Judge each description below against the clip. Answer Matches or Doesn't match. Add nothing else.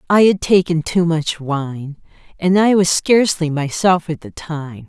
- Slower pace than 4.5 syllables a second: Matches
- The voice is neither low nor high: Matches